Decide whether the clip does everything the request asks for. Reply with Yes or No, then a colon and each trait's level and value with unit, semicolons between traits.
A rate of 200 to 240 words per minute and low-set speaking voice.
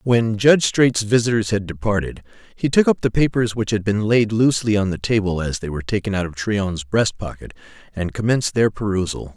Yes: fast, 205 wpm; low, 110 Hz